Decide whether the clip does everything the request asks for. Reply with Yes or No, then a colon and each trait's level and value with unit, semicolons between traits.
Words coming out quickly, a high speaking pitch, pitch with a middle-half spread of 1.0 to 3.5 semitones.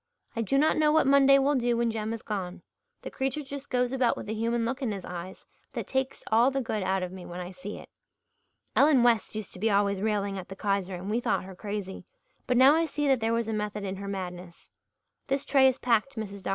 No: fast, 250 wpm; high, 220 Hz; average, 5.2 semitones